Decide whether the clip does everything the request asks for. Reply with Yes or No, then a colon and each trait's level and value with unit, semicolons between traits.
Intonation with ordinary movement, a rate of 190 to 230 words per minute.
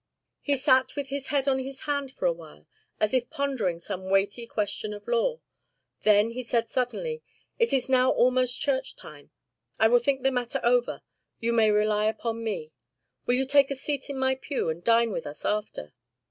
Yes: average, 4.2 semitones; average, 195 wpm